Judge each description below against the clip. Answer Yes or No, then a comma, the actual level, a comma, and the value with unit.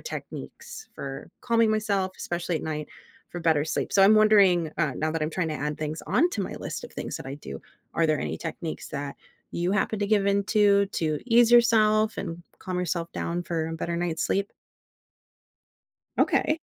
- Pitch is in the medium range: Yes, medium, 175 Hz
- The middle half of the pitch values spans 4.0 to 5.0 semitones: Yes, average, 4.6 semitones